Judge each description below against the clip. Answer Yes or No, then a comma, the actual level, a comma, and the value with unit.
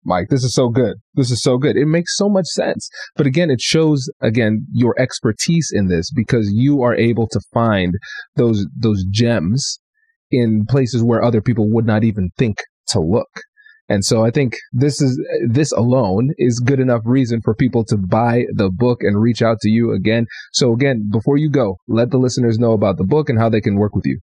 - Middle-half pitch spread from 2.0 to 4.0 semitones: Yes, average, 3.7 semitones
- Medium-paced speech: No, fast, 215 wpm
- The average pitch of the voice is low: Yes, low, 120 Hz